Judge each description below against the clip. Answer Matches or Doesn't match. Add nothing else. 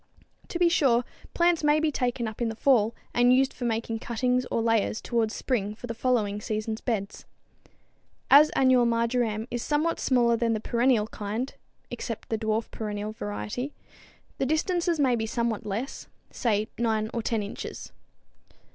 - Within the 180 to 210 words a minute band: Doesn't match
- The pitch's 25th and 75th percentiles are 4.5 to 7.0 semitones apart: Doesn't match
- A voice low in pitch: Doesn't match